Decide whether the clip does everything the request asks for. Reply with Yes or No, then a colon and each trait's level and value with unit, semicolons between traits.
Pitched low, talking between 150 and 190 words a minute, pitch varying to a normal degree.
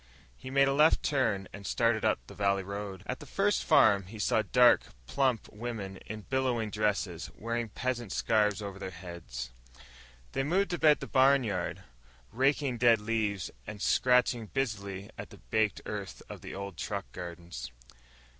Yes: low, 110 Hz; average, 160 wpm; average, 4.3 semitones